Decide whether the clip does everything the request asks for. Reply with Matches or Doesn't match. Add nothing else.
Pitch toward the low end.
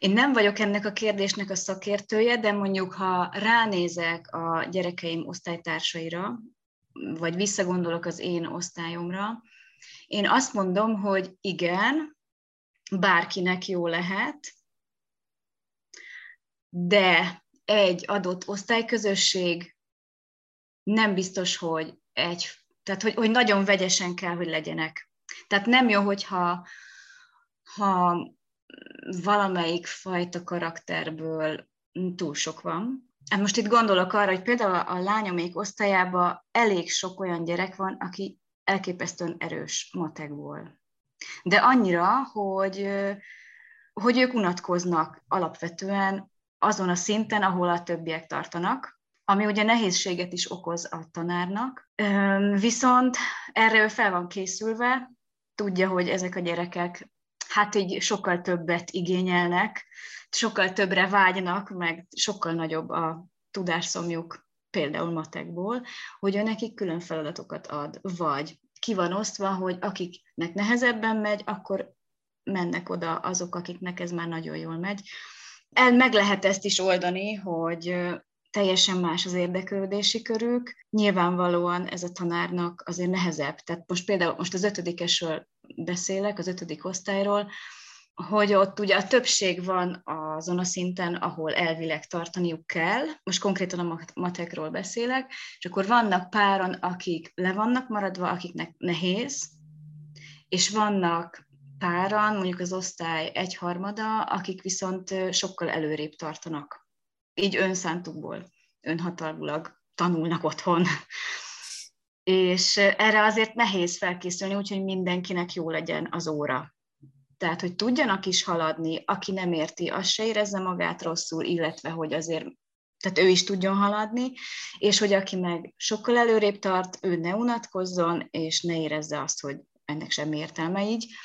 Doesn't match